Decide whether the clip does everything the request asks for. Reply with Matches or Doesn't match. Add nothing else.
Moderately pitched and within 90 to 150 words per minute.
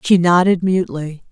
Matches